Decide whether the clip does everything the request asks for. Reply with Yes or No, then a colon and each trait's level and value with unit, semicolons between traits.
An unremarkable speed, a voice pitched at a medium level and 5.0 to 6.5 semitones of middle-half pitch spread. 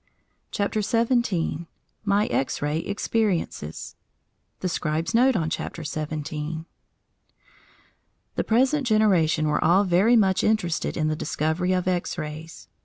No: slow, 120 wpm; medium, 175 Hz; wide, 5.4 semitones